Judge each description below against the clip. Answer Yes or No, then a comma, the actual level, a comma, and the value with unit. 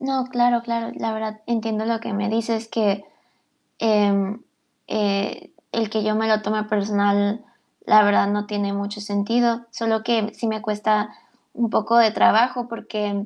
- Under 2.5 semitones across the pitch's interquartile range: Yes, narrow, 1.9 semitones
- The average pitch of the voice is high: Yes, high, 215 Hz